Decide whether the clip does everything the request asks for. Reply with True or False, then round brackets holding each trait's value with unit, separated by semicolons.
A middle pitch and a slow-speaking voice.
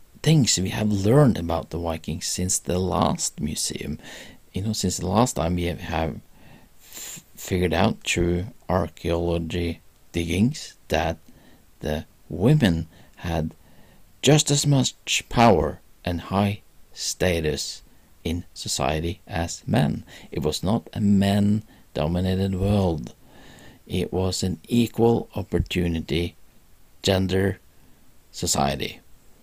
False (90 Hz; 110 wpm)